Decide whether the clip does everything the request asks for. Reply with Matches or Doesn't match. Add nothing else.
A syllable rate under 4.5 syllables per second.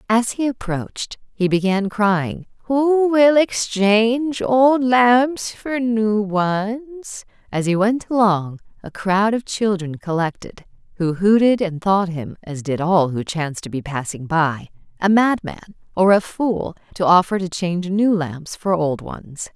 Matches